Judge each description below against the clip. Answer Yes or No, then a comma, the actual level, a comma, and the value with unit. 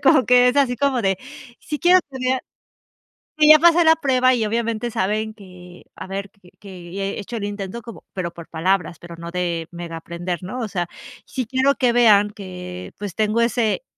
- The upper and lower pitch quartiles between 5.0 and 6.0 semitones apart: Yes, wide, 5.6 semitones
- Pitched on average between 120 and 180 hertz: No, high, 210 Hz